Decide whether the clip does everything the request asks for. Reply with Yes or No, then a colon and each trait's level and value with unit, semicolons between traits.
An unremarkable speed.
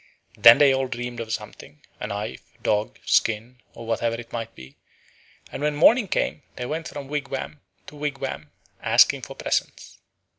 Yes: average, 160 wpm